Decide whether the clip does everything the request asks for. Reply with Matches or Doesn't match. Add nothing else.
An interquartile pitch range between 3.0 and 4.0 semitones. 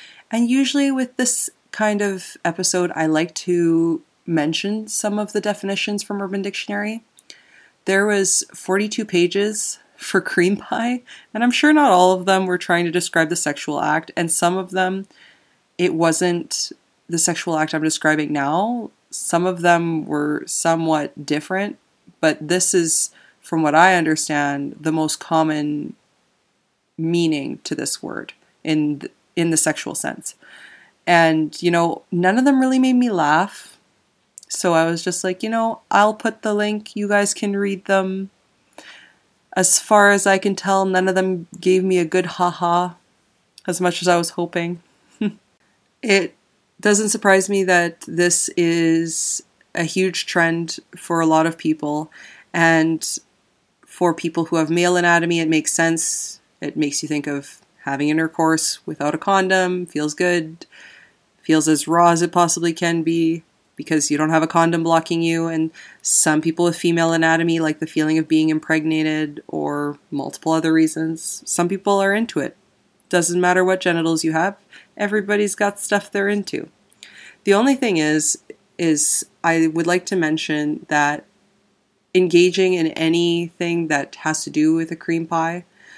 Matches